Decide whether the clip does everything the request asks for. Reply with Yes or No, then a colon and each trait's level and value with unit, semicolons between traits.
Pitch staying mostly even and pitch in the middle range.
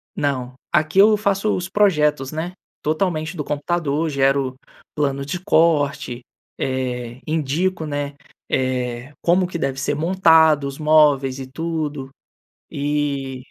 No: average, 3.4 semitones; medium, 150 Hz